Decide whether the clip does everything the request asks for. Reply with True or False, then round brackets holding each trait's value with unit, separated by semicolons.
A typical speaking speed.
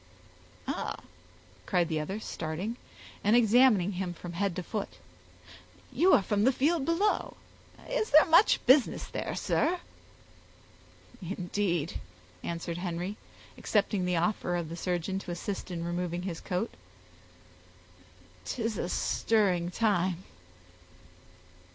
False (120 wpm)